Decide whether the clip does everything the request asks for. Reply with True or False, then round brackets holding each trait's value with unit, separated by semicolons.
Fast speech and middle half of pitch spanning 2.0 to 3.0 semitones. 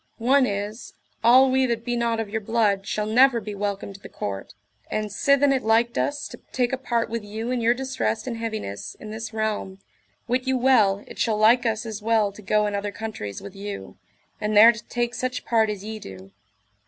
True (215 wpm; 2.7 semitones)